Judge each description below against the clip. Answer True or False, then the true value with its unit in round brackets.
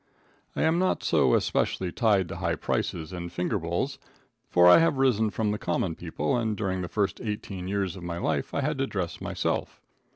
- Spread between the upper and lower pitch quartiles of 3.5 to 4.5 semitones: True (4.2 semitones)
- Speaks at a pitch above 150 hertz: False (95 Hz)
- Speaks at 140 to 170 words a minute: False (200 wpm)